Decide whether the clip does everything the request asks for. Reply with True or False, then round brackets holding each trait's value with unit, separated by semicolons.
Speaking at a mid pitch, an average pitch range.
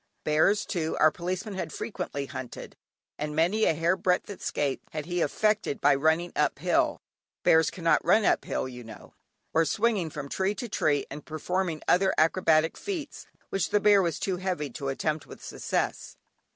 True (165 Hz; 4.0 semitones)